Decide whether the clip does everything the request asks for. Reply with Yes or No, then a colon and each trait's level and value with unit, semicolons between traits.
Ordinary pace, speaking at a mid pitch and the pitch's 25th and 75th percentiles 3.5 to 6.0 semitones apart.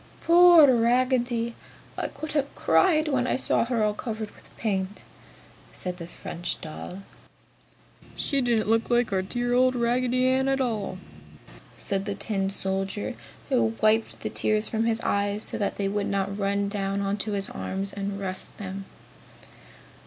No: average, 160 wpm; high, 215 Hz; average, 3.9 semitones